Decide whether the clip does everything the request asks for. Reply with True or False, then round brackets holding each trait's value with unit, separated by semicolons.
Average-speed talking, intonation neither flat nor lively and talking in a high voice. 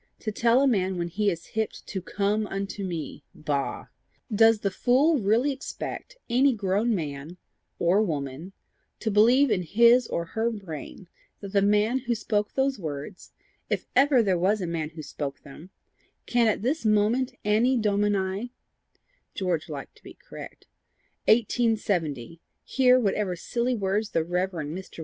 True (155 wpm; 4.8 semitones; 205 Hz)